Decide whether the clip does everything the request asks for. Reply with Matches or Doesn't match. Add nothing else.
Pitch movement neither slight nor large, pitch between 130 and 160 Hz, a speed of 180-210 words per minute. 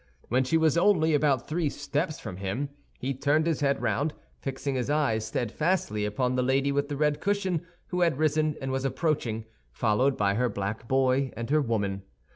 Matches